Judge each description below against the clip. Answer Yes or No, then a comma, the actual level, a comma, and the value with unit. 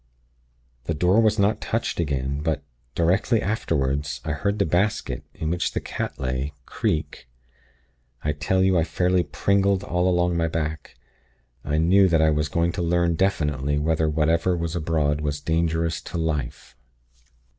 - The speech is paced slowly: No, average, 155 wpm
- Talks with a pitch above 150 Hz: No, very low, 80 Hz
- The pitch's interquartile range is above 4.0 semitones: No, average, 3.2 semitones